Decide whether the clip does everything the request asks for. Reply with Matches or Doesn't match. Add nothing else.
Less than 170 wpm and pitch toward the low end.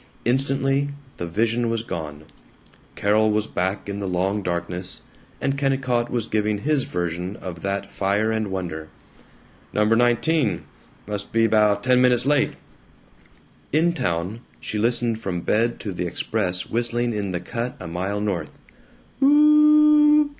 Matches